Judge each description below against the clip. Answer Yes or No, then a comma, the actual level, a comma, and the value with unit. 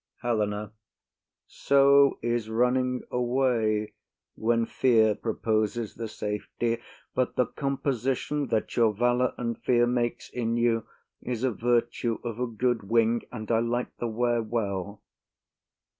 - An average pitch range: No, narrow, 1.8 semitones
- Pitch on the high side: No, low, 120 Hz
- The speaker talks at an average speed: No, slow, 130 wpm